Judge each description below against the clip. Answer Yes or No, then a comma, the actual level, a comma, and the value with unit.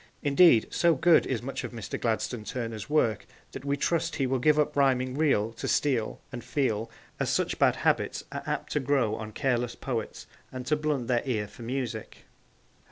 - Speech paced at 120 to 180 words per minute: No, average, 190 wpm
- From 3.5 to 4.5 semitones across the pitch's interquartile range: Yes, average, 3.8 semitones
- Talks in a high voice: No, low, 130 Hz